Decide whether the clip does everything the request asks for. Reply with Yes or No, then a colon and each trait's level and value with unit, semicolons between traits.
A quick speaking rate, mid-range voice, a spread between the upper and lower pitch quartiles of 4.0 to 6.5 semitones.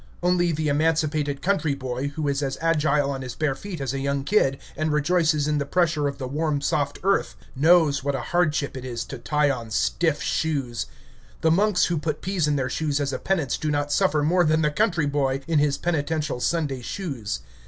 No: fast, 210 wpm; medium, 150 Hz; average, 2.8 semitones